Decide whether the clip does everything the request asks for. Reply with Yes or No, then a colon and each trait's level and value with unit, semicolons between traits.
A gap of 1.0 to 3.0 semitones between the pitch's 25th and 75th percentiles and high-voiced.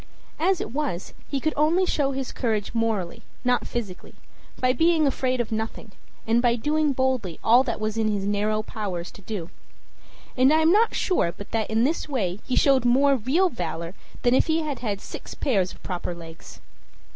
No: average, 5.3 semitones; high, 240 Hz